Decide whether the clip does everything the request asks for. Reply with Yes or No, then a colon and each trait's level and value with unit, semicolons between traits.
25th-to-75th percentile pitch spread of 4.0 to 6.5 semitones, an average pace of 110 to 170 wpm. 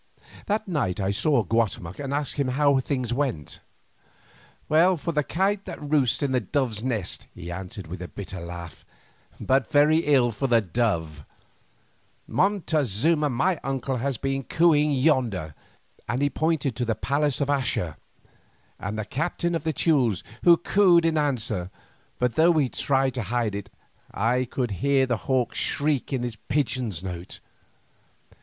Yes: average, 5.3 semitones; average, 160 wpm